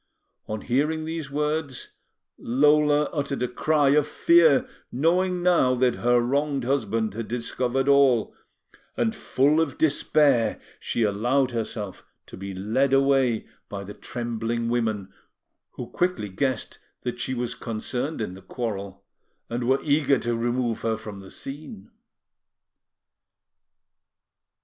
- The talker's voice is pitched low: Yes, low, 125 Hz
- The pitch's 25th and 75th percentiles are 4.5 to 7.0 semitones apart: No, average, 4.0 semitones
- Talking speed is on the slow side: Yes, slow, 130 wpm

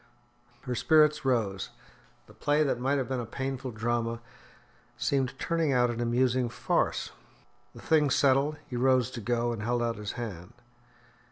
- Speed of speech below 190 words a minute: Yes, average, 160 wpm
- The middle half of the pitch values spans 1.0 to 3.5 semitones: Yes, narrow, 2.5 semitones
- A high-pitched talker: No, low, 125 Hz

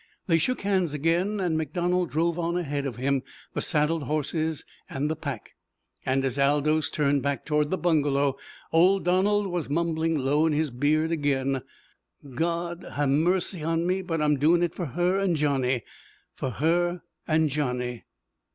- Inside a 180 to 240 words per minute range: No, average, 165 wpm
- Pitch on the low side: No, medium, 155 Hz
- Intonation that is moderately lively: Yes, average, 3.4 semitones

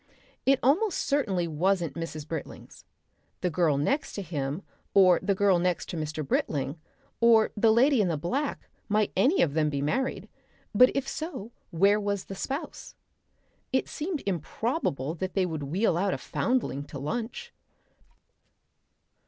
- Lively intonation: Yes, wide, 7.3 semitones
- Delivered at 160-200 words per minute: No, average, 150 wpm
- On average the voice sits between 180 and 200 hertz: Yes, high, 190 Hz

